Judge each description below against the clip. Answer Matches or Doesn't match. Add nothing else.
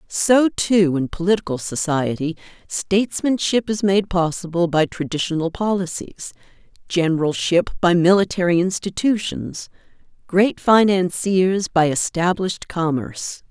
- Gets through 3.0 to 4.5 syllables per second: Matches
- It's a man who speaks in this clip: Doesn't match